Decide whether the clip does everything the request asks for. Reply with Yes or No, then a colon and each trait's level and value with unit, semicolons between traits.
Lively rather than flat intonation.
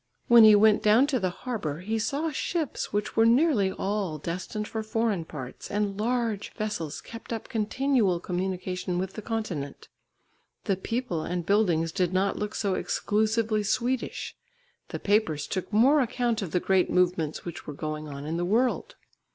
No: average, 4.3 semitones